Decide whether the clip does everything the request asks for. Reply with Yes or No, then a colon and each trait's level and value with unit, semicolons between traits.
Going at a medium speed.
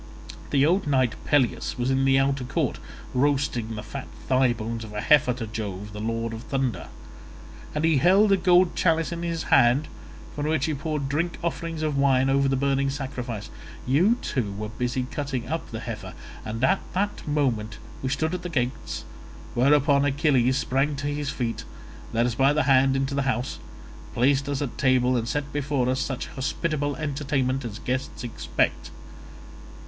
Yes: average, 180 wpm